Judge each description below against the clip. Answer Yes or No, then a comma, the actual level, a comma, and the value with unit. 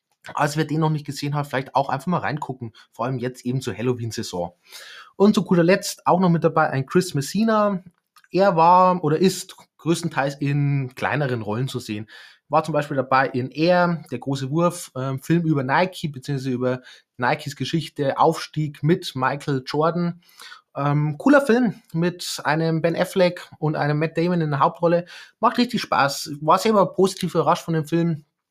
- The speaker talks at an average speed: Yes, average, 175 wpm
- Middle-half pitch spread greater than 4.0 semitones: Yes, average, 4.5 semitones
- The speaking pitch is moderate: Yes, medium, 155 Hz